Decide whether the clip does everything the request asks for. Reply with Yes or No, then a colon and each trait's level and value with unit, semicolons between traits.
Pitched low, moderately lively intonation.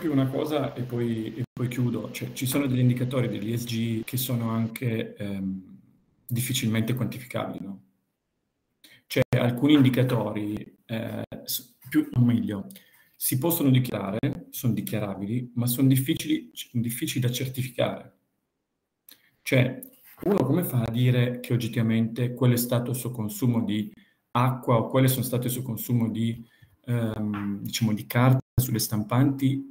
No: low, 120 Hz; narrow, 2.3 semitones